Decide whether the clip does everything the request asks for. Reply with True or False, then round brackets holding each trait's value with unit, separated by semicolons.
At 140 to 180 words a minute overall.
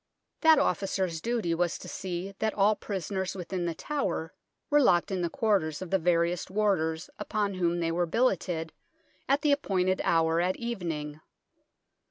True (160 wpm)